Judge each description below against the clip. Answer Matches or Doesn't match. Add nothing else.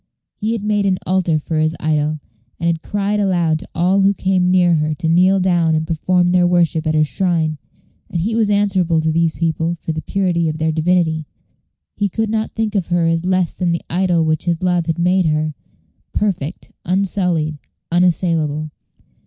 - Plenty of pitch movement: Doesn't match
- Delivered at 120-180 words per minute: Doesn't match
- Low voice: Doesn't match